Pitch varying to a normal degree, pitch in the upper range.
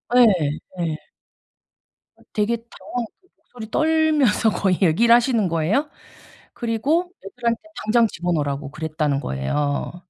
No: wide, 7.3 semitones; high, 220 Hz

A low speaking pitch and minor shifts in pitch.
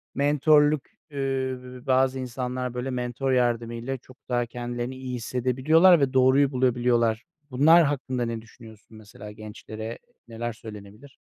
Yes: low, 125 Hz; narrow, 2.2 semitones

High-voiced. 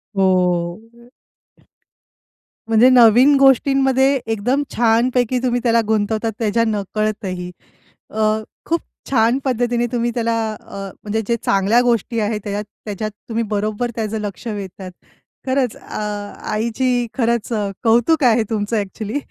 Yes: high, 225 Hz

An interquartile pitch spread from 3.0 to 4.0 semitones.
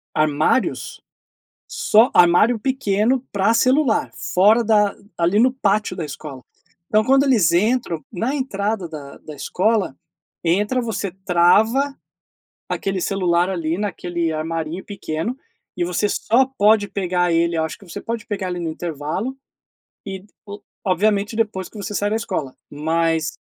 No: average, 4.7 semitones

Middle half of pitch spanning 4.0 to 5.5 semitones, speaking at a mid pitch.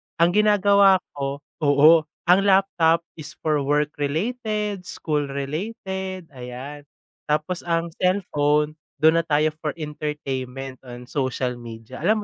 Yes: average, 4.7 semitones; medium, 155 Hz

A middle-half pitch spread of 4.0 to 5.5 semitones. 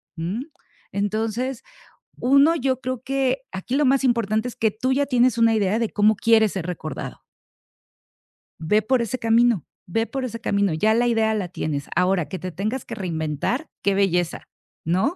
Yes: average, 4.8 semitones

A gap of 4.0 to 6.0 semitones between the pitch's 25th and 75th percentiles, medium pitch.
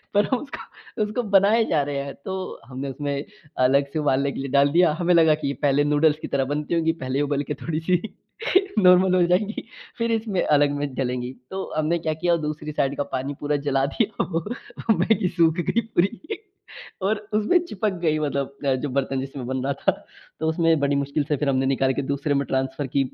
Yes: average, 4.3 semitones; medium, 150 Hz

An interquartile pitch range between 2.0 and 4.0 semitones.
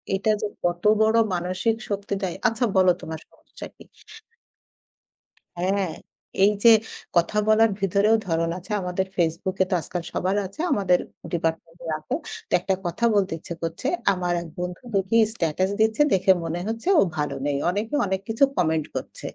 Yes: average, 3.2 semitones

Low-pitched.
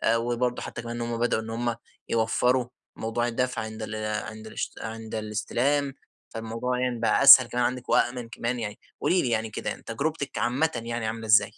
Yes: low, 120 Hz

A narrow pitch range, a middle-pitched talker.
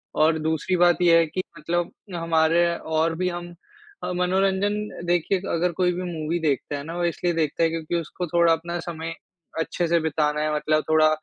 Yes: narrow, 1.7 semitones; medium, 165 Hz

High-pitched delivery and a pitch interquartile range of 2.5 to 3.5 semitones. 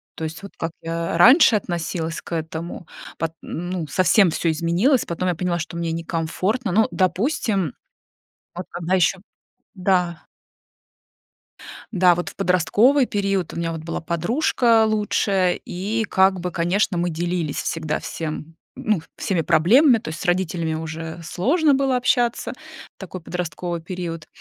No: medium, 175 Hz; average, 3.1 semitones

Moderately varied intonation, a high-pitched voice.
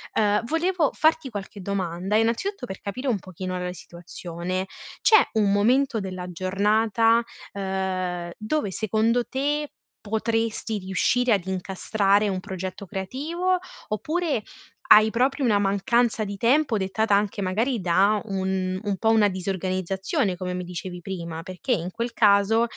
Yes: average, 3.7 semitones; high, 205 Hz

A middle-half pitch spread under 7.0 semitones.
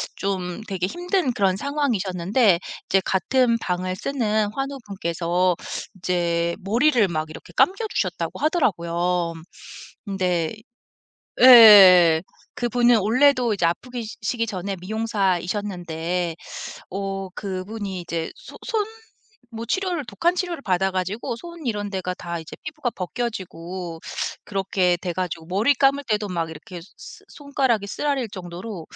Yes: average, 5.2 semitones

